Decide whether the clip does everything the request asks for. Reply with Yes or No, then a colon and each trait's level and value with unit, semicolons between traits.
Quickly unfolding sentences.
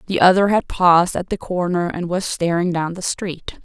Yes: fast, 215 wpm